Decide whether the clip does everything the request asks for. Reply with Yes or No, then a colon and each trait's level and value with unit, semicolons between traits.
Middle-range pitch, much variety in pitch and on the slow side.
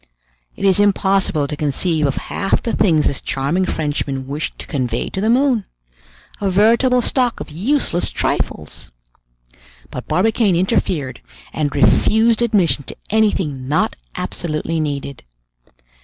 Yes: medium, 180 Hz; wide, 6.8 semitones; slow, 130 wpm